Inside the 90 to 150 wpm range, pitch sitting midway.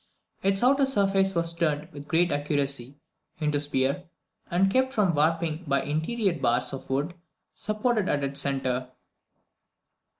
Yes: average, 140 wpm; medium, 160 Hz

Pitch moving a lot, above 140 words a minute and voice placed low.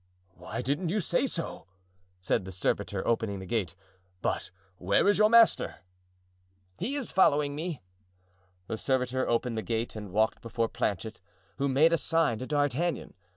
Yes: wide, 7.0 semitones; average, 155 wpm; low, 130 Hz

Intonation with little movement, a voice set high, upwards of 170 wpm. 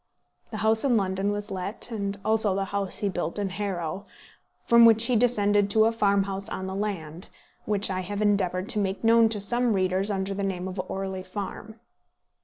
Yes: narrow, 2.2 semitones; high, 200 Hz; average, 195 wpm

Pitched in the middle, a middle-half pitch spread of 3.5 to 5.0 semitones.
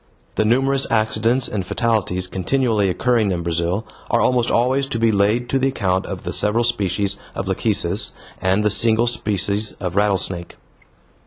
No: low, 105 Hz; average, 3.8 semitones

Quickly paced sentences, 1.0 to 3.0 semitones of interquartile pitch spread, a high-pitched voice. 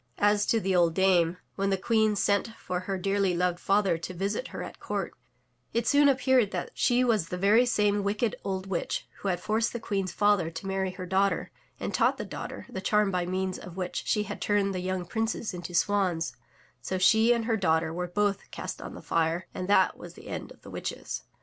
Yes: fast, 220 wpm; narrow, 2.5 semitones; high, 195 Hz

